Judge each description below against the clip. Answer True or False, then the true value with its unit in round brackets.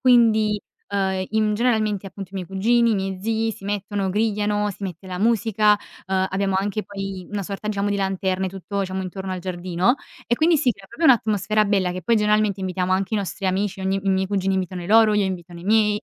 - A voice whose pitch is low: False (200 Hz)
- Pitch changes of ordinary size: False (2.0 semitones)